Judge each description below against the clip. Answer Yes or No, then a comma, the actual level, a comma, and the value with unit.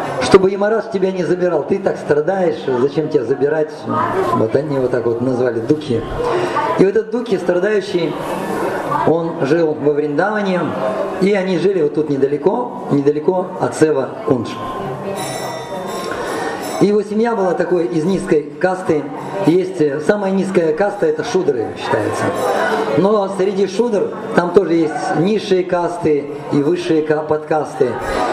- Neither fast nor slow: Yes, average, 140 wpm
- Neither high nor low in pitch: Yes, medium, 175 Hz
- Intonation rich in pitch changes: No, average, 4.7 semitones